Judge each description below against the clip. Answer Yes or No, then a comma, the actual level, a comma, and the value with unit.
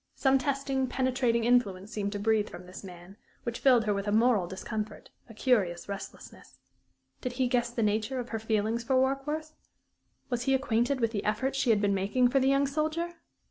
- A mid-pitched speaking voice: No, high, 235 Hz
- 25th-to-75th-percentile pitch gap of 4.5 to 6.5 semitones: No, average, 4.1 semitones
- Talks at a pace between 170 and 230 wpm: Yes, average, 195 wpm